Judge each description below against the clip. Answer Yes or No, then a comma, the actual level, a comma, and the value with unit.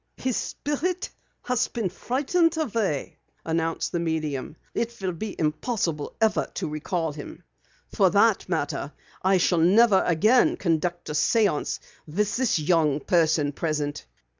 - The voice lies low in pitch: No, medium, 180 Hz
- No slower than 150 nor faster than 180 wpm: No, slow, 135 wpm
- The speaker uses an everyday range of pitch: No, wide, 6.7 semitones